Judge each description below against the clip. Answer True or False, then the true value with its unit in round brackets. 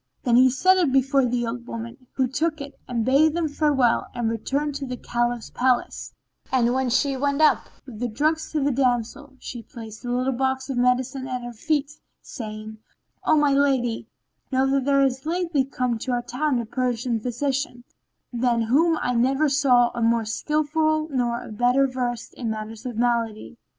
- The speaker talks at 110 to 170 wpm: False (185 wpm)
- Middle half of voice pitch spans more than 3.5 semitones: False (2.8 semitones)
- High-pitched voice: True (255 Hz)